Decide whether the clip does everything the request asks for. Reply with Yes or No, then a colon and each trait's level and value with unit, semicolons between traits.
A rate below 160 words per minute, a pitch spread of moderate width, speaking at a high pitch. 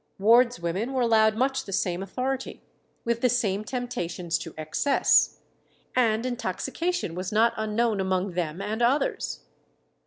Yes: slow, 135 wpm; average, 4.7 semitones; high, 220 Hz